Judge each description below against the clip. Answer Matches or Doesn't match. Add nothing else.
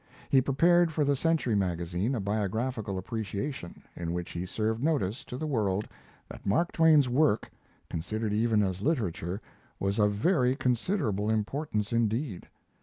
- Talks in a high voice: Doesn't match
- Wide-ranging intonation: Matches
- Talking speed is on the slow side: Doesn't match